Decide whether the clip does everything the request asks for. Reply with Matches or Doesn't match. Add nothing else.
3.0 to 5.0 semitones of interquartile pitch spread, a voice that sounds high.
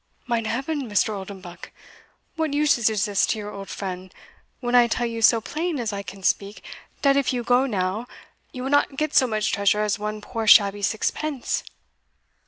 Matches